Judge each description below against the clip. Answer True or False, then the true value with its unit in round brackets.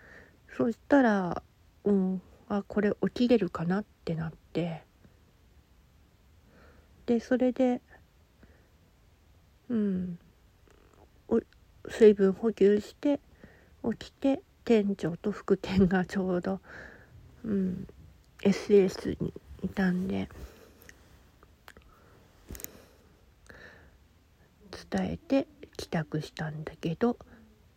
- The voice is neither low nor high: True (175 Hz)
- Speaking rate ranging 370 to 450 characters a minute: False (145 characters per minute)